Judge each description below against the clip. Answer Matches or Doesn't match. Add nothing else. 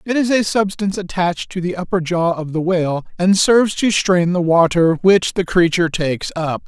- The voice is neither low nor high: Matches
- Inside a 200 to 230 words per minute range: Matches